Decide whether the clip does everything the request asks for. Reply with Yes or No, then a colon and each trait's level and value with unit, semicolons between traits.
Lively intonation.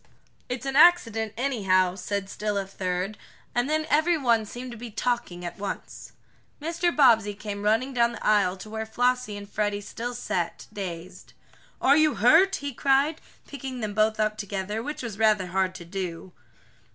No: average, 4.3 semitones